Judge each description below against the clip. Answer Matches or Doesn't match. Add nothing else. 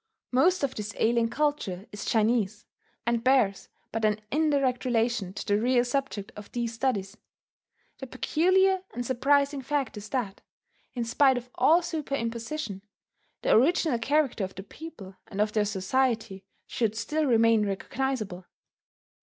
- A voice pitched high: Matches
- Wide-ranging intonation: Doesn't match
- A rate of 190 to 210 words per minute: Doesn't match